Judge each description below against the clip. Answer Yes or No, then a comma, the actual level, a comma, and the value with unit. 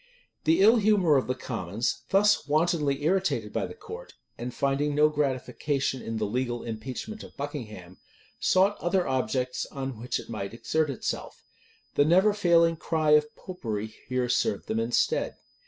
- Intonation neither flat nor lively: No, wide, 5.8 semitones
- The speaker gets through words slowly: No, average, 160 wpm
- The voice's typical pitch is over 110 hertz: Yes, medium, 140 Hz